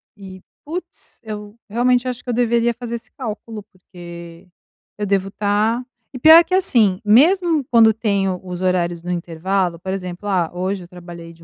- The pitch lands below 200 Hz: No, high, 205 Hz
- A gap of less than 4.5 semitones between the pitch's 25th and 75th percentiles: No, average, 4.8 semitones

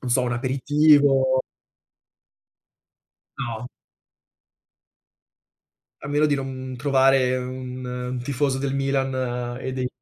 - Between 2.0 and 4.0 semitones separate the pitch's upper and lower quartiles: No, narrow, 1.3 semitones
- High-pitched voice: No, low, 130 Hz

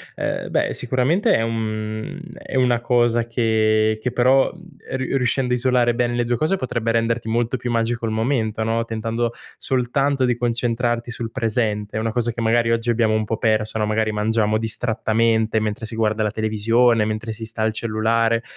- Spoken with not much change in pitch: Yes, narrow, 1.7 semitones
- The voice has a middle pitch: No, low, 115 Hz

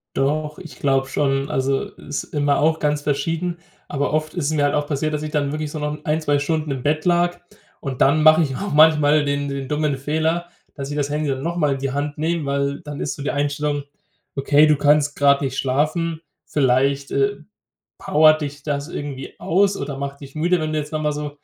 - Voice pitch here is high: No, medium, 145 Hz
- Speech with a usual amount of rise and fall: No, narrow, 1.7 semitones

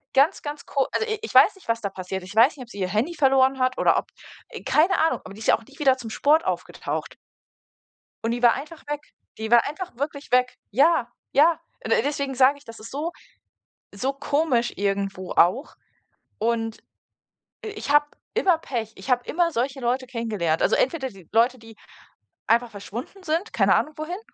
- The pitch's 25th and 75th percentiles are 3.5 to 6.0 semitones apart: Yes, average, 4.6 semitones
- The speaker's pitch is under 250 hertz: No, very high, 260 Hz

